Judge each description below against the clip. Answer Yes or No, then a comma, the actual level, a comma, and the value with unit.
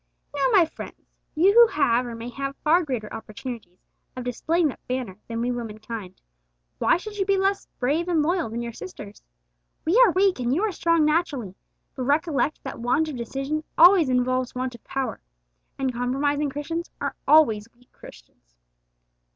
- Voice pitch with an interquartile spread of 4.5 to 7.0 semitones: Yes, wide, 5.5 semitones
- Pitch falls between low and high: No, very high, 270 Hz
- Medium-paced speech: Yes, average, 175 wpm